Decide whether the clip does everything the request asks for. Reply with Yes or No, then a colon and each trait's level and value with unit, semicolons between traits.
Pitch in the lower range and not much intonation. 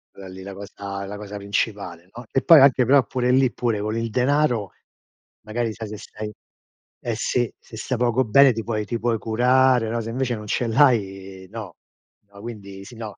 No: low, 115 Hz; average, 3.3 semitones